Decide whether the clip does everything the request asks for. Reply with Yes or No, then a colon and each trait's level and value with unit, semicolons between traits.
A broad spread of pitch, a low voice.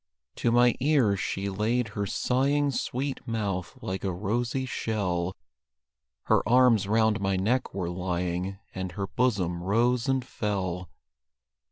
No: average, 4.7 semitones; low, 105 Hz